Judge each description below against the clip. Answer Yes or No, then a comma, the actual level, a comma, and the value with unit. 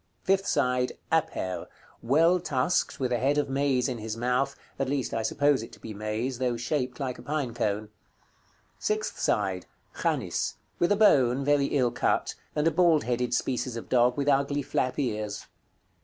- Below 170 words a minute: No, average, 175 wpm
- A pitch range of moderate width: Yes, average, 3.3 semitones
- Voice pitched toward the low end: Yes, low, 130 Hz